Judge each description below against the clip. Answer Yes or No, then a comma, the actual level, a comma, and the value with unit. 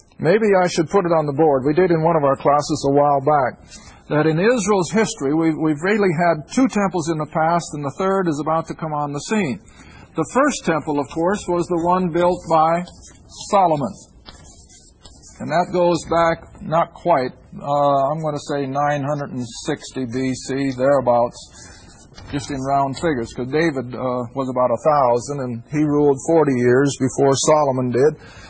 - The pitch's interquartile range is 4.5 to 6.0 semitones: No, average, 3.8 semitones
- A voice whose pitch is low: No, medium, 150 Hz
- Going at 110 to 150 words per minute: No, average, 180 wpm